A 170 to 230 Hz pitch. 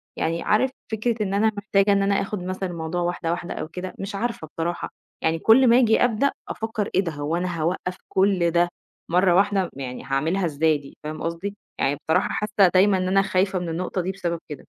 Yes: medium, 185 Hz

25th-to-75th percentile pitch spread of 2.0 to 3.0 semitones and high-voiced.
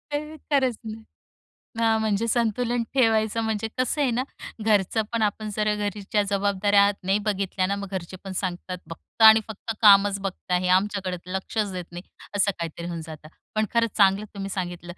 Yes: average, 2.7 semitones; high, 205 Hz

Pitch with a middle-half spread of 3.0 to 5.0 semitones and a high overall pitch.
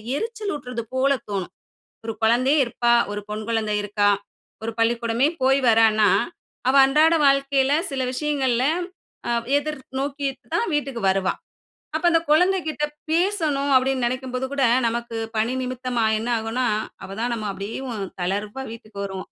Yes: average, 3.8 semitones; very high, 255 Hz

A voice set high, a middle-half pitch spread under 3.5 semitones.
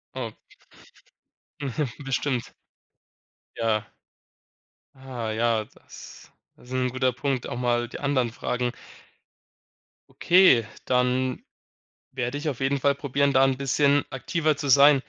No: low, 130 Hz; narrow, 2.5 semitones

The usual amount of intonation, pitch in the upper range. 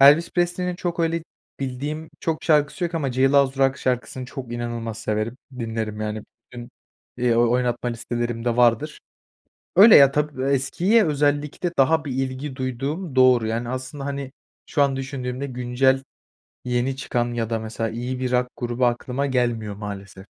No: average, 3.0 semitones; low, 130 Hz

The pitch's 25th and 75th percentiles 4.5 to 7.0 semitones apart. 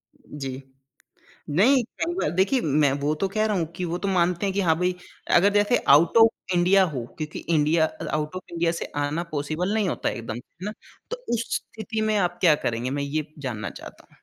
Yes: average, 5.2 semitones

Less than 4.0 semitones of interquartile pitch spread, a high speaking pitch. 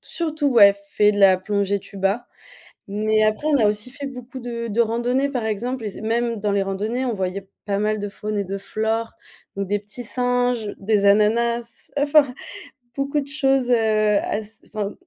Yes: average, 3.3 semitones; high, 220 Hz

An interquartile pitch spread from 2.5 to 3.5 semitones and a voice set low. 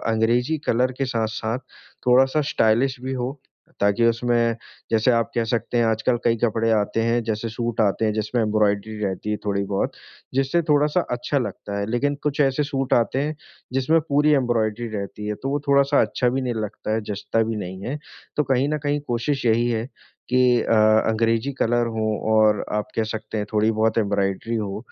Yes: average, 3.1 semitones; low, 115 Hz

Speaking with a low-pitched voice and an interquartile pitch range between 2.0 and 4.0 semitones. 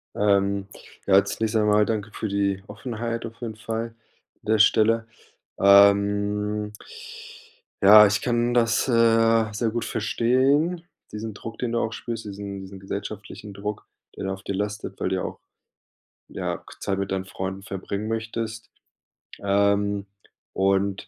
Yes: low, 105 Hz; narrow, 2.4 semitones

